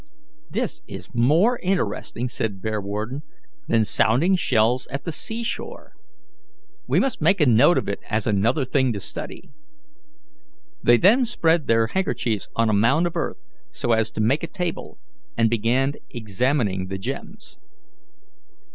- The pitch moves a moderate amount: No, wide, 6.9 semitones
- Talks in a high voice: No, low, 120 Hz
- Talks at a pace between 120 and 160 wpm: Yes, average, 145 wpm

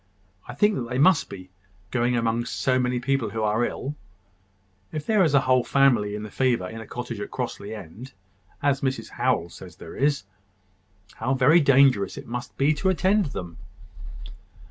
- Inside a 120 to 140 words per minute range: No, average, 175 wpm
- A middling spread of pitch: Yes, average, 3.9 semitones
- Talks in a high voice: No, low, 125 Hz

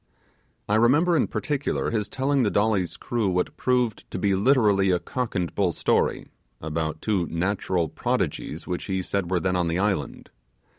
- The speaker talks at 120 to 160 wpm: No, average, 170 wpm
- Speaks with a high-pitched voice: No, low, 100 Hz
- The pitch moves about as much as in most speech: Yes, average, 4.6 semitones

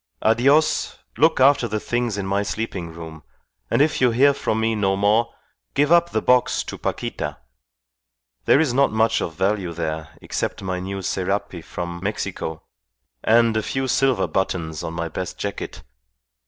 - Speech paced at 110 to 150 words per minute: No, average, 165 wpm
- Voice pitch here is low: Yes, low, 105 Hz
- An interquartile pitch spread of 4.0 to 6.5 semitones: Yes, average, 5.1 semitones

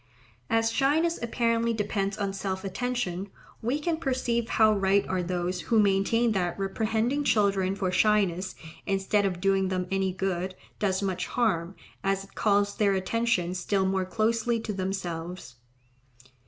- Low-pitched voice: No, high, 195 Hz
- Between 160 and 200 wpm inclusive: No, average, 145 wpm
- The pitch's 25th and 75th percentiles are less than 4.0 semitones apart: Yes, average, 3.2 semitones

